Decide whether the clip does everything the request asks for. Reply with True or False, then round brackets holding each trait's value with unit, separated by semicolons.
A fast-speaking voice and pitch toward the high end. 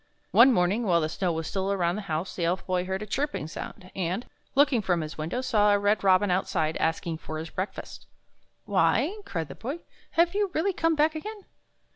True (215 wpm; 195 Hz)